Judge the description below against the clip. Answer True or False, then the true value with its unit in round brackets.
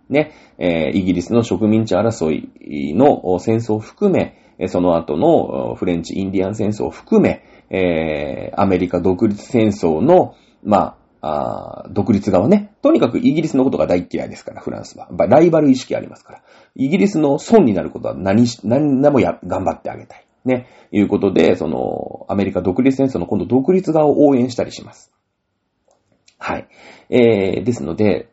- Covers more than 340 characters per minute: False (330 characters per minute)